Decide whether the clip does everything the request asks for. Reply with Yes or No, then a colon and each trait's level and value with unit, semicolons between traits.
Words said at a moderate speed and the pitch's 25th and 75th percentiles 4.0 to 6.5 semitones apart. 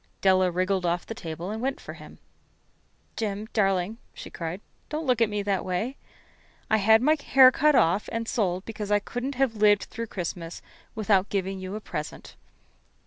No: average, 180 wpm; average, 3.5 semitones